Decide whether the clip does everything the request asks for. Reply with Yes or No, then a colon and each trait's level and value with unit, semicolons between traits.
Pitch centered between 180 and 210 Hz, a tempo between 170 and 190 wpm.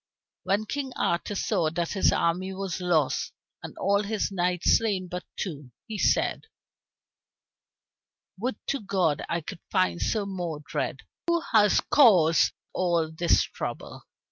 No: medium, 185 Hz; slow, 135 wpm